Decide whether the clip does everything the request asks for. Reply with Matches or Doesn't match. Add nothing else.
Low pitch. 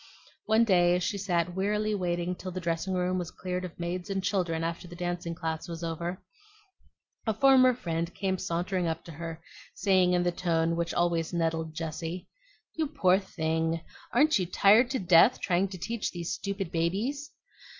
Doesn't match